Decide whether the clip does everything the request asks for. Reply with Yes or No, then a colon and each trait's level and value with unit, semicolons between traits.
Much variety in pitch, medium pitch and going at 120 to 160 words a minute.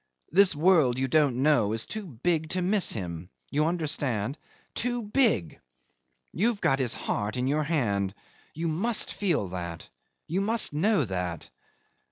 Yes: wide, 8.7 semitones; medium, 150 Hz; average, 150 wpm